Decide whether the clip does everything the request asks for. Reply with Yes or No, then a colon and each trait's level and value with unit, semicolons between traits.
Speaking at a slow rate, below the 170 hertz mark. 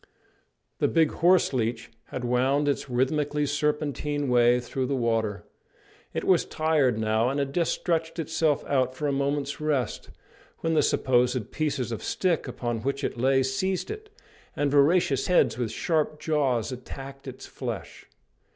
No: average, 155 wpm; medium, 140 Hz